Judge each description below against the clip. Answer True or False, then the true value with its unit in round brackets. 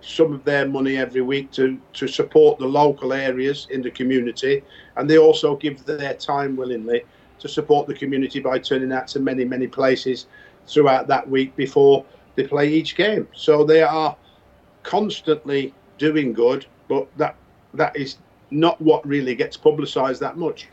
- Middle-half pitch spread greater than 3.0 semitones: False (2.7 semitones)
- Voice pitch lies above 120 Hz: True (140 Hz)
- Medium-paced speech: True (170 wpm)